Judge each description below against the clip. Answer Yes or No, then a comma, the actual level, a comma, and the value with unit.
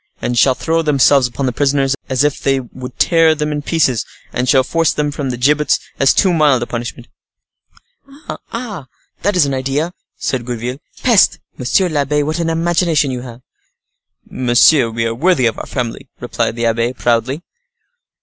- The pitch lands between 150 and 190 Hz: No, low, 135 Hz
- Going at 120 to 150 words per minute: No, average, 175 wpm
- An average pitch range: Yes, average, 4.2 semitones